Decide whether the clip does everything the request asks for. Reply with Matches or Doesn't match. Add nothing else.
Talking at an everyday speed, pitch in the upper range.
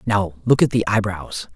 Doesn't match